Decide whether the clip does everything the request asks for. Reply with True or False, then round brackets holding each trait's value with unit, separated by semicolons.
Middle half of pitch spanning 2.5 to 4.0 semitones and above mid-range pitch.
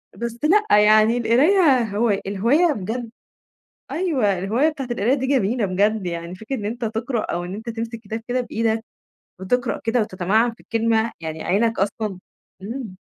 True (3.3 semitones; 225 Hz)